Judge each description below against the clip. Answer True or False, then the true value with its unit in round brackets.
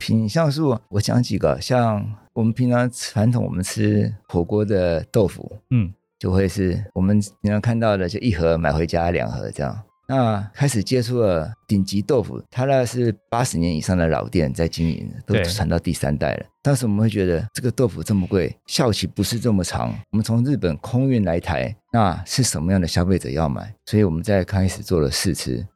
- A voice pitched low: True (105 Hz)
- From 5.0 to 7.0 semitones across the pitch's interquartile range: False (4.2 semitones)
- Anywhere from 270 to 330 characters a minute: True (295 characters per minute)